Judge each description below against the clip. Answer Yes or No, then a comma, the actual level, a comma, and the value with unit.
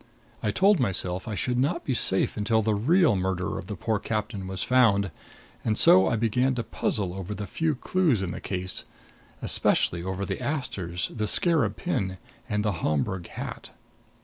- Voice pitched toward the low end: Yes, low, 105 Hz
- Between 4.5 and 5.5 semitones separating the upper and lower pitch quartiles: Yes, average, 4.8 semitones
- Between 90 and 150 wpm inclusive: No, average, 175 wpm